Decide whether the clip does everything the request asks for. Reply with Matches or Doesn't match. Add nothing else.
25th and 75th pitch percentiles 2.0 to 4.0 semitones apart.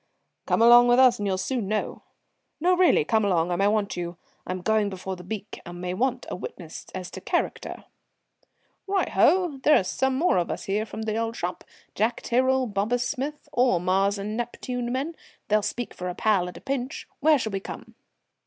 Doesn't match